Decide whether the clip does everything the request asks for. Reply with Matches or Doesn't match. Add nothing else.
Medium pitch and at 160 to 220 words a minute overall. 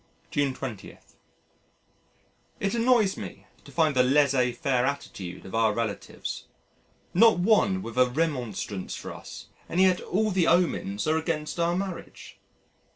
Doesn't match